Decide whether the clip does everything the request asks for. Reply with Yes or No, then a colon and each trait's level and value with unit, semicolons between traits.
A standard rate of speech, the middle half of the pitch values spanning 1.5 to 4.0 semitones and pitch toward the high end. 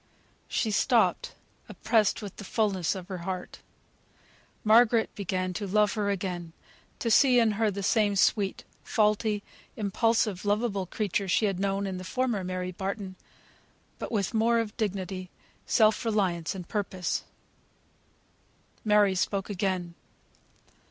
No: slow, 130 wpm; narrow, 2.6 semitones; high, 200 Hz